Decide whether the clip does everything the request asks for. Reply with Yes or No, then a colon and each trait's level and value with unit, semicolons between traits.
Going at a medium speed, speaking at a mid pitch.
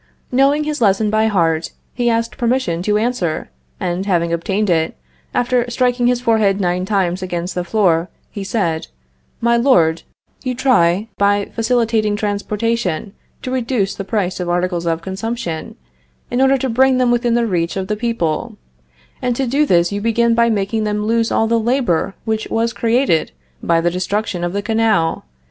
No: average, 170 wpm; high, 210 Hz